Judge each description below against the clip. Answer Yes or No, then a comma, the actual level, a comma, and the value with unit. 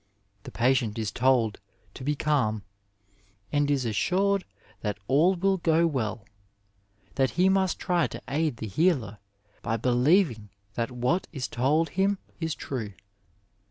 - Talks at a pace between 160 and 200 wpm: No, average, 145 wpm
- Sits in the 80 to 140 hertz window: Yes, low, 135 Hz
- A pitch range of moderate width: No, wide, 6.6 semitones